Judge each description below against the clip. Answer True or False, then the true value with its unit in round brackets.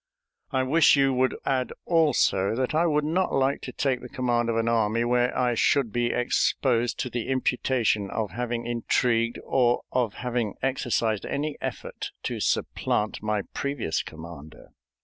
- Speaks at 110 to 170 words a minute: True (160 wpm)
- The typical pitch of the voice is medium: False (120 Hz)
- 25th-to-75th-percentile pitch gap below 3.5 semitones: True (2.7 semitones)